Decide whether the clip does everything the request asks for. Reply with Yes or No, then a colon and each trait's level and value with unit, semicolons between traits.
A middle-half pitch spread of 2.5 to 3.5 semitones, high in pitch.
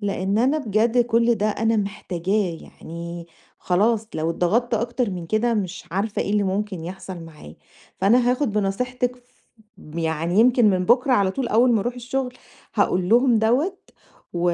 No: average, 4.7 semitones; high, 210 Hz